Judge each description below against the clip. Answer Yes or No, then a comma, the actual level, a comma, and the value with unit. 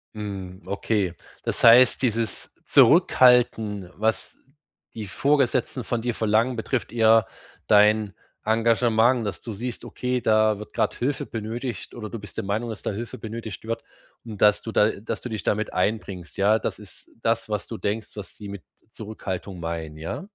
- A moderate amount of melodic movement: No, narrow, 2.2 semitones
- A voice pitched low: Yes, low, 110 Hz